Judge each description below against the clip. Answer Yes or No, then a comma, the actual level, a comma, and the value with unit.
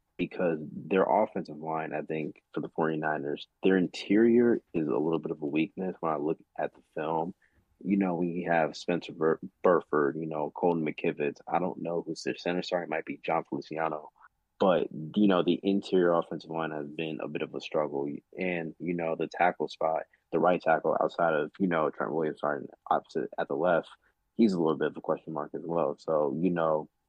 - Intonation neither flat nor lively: No, narrow, 2.3 semitones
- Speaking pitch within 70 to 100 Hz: Yes, very low, 80 Hz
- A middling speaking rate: No, fast, 210 wpm